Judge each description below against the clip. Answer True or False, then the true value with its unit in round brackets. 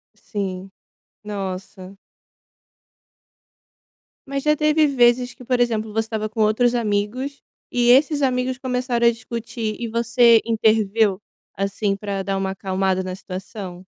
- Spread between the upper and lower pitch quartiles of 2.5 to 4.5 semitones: True (3.8 semitones)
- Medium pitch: False (220 Hz)